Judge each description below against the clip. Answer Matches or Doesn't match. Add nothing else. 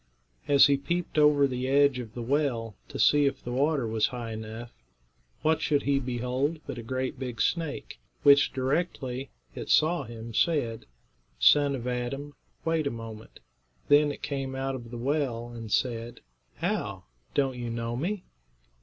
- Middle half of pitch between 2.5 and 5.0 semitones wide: Matches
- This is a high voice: Doesn't match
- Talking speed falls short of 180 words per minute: Matches